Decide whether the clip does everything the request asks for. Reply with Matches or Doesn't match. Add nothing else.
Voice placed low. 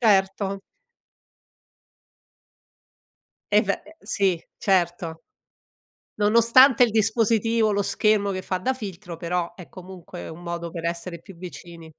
Doesn't match